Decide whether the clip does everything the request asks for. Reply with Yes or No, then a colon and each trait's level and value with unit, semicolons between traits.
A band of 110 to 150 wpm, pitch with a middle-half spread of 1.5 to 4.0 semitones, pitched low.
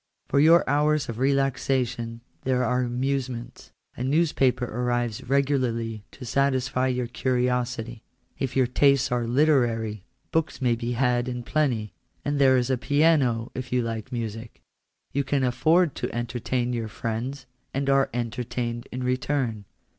Yes: average, 145 wpm; narrow, 2.5 semitones; low, 125 Hz